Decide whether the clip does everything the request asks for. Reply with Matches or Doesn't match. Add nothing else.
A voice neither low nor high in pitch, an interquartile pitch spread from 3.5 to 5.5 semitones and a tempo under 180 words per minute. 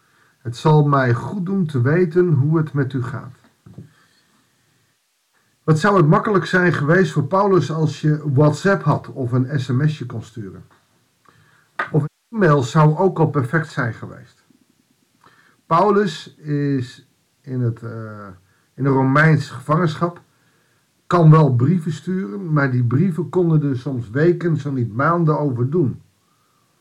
Matches